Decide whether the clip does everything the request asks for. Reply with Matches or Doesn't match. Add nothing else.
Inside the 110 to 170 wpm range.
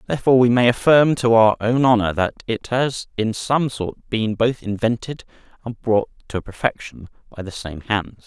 Doesn't match